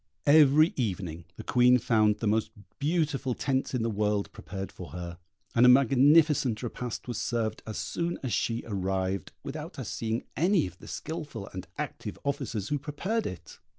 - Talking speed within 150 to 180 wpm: Yes, average, 170 wpm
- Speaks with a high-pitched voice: No, low, 120 Hz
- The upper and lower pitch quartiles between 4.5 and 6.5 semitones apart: Yes, wide, 5.6 semitones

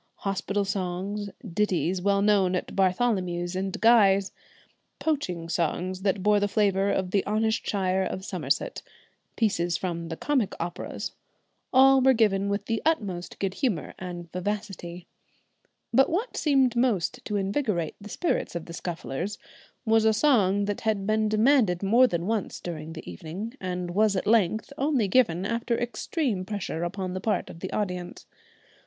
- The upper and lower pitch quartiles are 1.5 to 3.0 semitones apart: No, average, 3.5 semitones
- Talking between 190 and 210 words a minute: No, average, 155 wpm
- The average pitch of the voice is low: No, high, 200 Hz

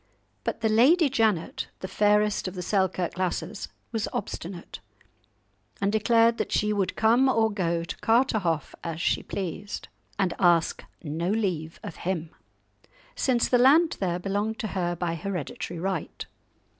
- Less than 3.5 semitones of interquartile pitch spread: No, average, 4.2 semitones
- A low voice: No, high, 195 Hz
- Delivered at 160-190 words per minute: No, average, 145 wpm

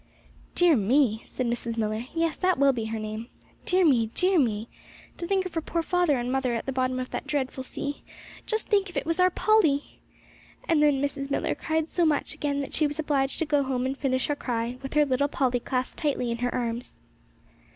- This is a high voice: Yes, very high, 275 Hz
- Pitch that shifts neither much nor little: Yes, average, 4.3 semitones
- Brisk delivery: Yes, fast, 220 wpm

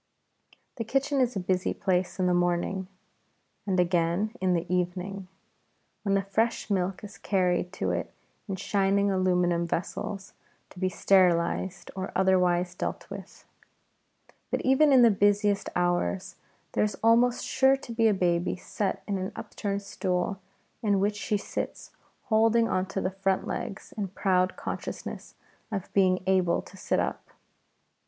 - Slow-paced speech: No, average, 150 wpm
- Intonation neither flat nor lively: No, narrow, 2.2 semitones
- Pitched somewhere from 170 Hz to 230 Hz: Yes, high, 190 Hz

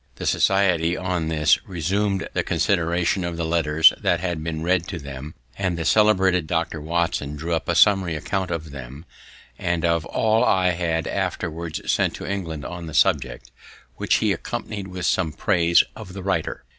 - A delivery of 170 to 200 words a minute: Yes, average, 175 wpm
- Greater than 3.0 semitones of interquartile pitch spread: No, narrow, 2.6 semitones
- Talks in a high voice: No, very low, 85 Hz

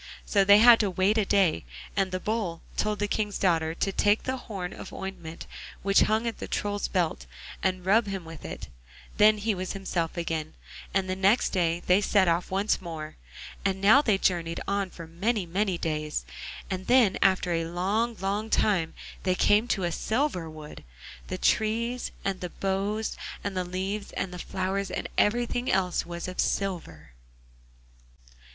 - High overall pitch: Yes, high, 195 Hz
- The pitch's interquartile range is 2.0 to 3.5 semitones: Yes, average, 3.0 semitones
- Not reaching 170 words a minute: No, average, 175 wpm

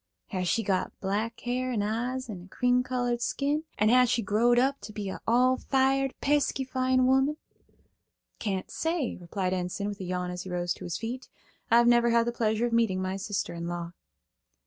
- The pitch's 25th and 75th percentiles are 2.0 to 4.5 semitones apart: No, average, 4.9 semitones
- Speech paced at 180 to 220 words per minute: Yes, average, 200 wpm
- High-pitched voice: Yes, high, 230 Hz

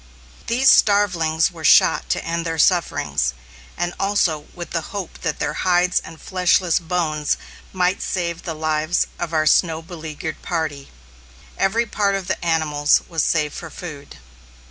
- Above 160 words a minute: No, average, 150 wpm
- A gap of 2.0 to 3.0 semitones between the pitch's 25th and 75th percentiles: Yes, narrow, 2.4 semitones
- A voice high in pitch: No, medium, 170 Hz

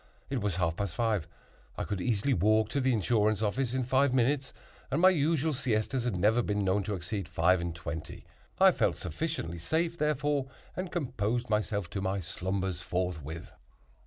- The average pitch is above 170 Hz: No, low, 110 Hz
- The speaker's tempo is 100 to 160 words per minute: No, average, 175 wpm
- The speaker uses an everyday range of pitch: No, wide, 6.1 semitones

